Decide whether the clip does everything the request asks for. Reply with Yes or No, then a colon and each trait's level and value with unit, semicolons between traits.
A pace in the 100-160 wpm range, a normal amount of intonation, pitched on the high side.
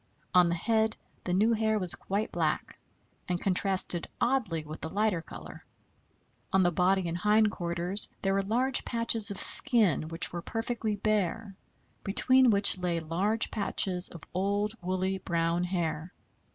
Yes: average, 150 wpm; average, 3.7 semitones; high, 195 Hz